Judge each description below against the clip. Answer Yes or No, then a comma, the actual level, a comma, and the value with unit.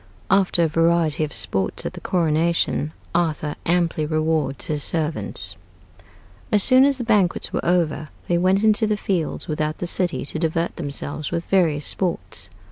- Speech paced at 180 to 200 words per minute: No, average, 160 wpm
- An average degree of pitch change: Yes, average, 3.0 semitones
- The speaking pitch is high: No, medium, 165 Hz